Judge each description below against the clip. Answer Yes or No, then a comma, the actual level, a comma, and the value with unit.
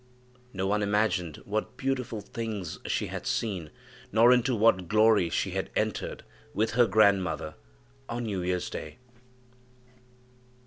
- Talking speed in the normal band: No, slow, 130 wpm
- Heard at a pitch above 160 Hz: No, low, 105 Hz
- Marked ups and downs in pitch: No, average, 3.5 semitones